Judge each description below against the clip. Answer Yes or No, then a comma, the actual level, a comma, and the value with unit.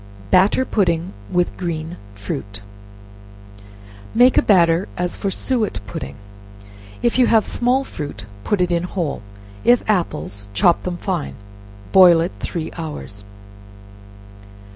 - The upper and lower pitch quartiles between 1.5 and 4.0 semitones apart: No, average, 4.5 semitones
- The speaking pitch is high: No, medium, 175 Hz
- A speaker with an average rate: No, slow, 120 wpm